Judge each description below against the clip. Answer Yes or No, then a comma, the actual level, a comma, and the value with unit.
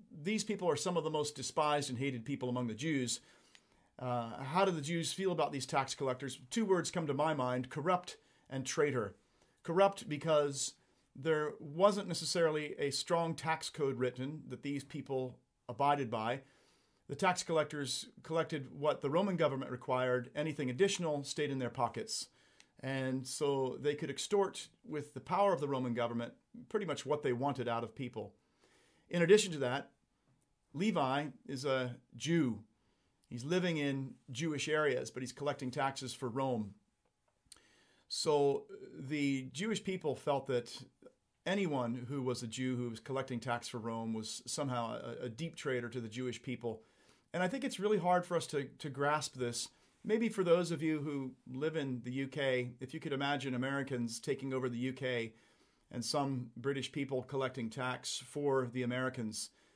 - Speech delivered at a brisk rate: No, average, 170 wpm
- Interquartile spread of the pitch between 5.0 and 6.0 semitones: No, average, 3.9 semitones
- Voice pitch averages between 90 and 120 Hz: No, medium, 140 Hz